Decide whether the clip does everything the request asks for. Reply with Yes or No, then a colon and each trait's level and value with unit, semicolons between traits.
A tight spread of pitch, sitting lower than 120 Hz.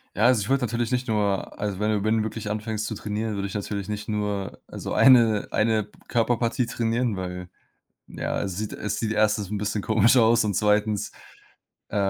Yes: narrow, 1.6 semitones; low, 105 Hz